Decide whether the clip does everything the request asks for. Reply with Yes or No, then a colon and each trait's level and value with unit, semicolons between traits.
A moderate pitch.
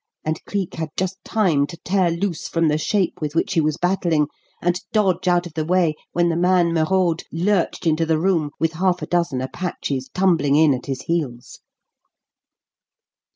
Yes: medium, 170 Hz